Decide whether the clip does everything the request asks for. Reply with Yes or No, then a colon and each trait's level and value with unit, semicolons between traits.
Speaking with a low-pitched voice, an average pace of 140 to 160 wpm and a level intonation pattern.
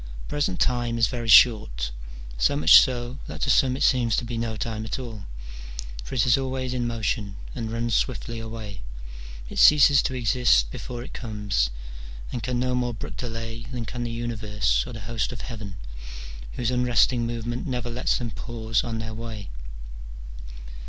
No: low, 115 Hz; average, 175 wpm; narrow, 2.0 semitones